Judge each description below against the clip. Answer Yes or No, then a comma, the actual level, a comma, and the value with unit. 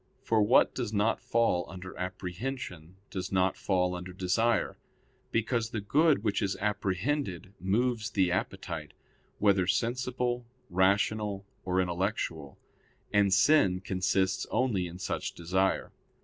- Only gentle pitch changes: No, average, 3.6 semitones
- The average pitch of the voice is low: Yes, very low, 95 Hz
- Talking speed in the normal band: No, slow, 120 wpm